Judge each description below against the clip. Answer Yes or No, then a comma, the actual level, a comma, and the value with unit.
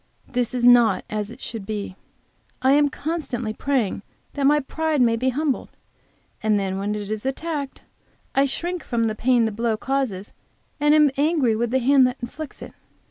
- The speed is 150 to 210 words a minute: Yes, average, 185 wpm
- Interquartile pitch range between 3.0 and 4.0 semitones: No, average, 4.5 semitones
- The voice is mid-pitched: No, very high, 250 Hz